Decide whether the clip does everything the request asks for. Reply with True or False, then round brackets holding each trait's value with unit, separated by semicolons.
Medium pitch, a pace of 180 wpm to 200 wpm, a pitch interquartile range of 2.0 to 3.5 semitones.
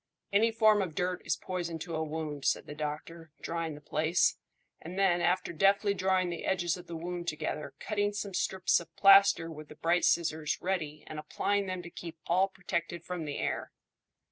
True (175 Hz; 195 wpm; 3.0 semitones)